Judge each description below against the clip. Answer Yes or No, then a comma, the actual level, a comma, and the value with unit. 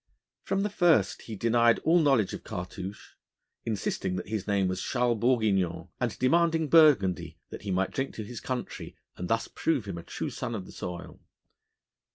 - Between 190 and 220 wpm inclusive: No, average, 180 wpm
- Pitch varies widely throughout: Yes, wide, 5.7 semitones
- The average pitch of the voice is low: Yes, low, 110 Hz